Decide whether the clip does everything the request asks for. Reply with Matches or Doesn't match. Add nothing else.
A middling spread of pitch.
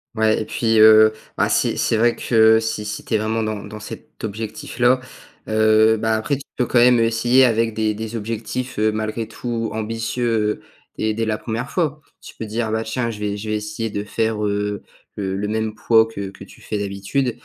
Doesn't match